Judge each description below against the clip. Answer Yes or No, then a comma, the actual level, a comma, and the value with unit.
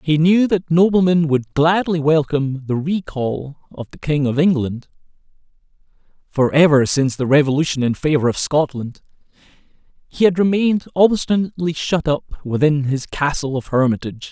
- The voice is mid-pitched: Yes, medium, 155 Hz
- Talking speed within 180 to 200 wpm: No, average, 145 wpm